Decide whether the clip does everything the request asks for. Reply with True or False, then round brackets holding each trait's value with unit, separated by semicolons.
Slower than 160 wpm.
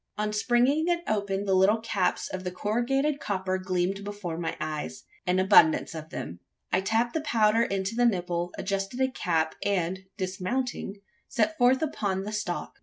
False (165 wpm)